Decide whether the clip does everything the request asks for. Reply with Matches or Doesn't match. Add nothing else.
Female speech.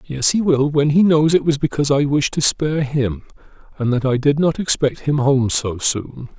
Doesn't match